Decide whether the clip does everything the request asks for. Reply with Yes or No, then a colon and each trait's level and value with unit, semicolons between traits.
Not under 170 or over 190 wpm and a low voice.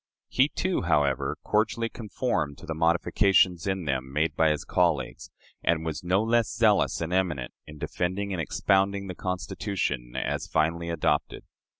No: average, 155 wpm; very low, 90 Hz